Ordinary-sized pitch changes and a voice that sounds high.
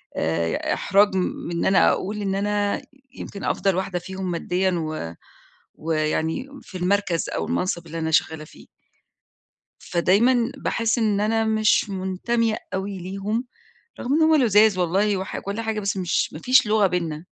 Yes: average, 3.5 semitones; high, 195 Hz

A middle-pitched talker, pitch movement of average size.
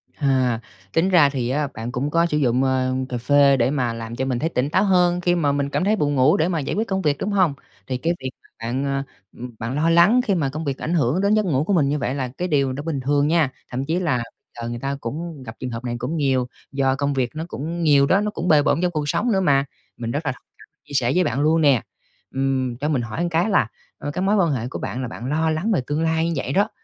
Yes: medium, 145 Hz; average, 4.3 semitones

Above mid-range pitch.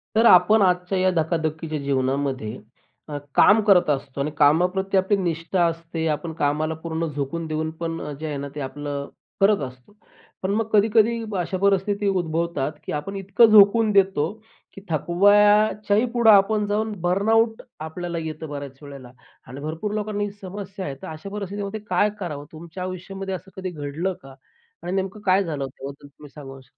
No: medium, 175 Hz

